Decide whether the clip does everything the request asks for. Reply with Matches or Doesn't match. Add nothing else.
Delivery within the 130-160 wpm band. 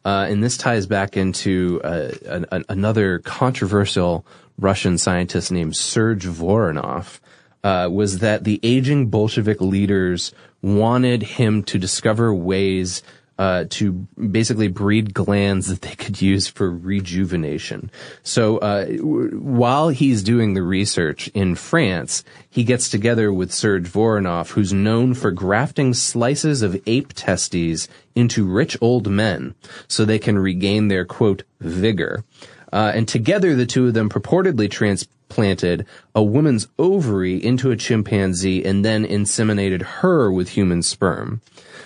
Matches